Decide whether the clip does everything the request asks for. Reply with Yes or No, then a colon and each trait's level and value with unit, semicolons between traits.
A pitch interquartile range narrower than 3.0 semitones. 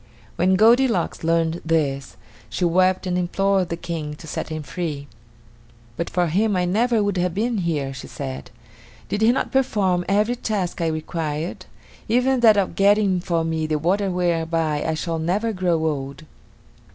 No: average, 4.0 semitones